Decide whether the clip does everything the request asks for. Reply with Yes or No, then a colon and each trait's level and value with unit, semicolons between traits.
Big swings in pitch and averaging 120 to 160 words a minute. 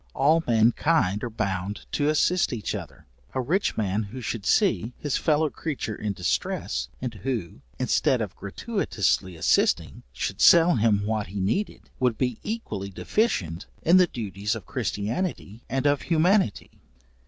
Yes: wide, 7.1 semitones; average, 150 wpm